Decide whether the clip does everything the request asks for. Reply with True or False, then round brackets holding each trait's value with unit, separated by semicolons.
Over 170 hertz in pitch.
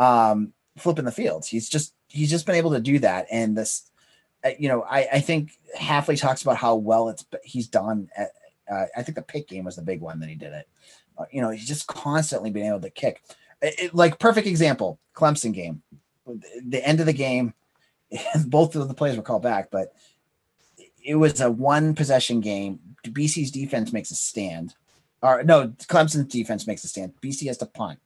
False (135 Hz)